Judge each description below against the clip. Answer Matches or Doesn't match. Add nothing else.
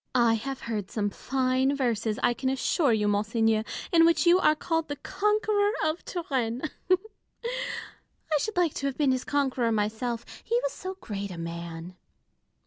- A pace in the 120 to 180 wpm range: Matches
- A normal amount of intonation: Doesn't match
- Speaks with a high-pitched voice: Matches